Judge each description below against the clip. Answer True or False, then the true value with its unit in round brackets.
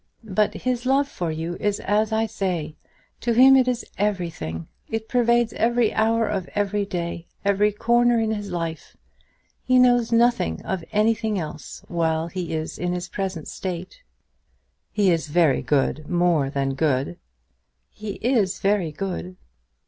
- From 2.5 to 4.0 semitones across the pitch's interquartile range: False (5.1 semitones)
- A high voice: True (195 Hz)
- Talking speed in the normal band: True (150 wpm)